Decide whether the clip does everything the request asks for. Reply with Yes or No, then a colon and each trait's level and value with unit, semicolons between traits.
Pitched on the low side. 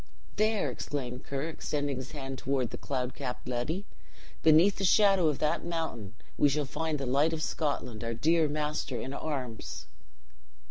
No: medium, 145 Hz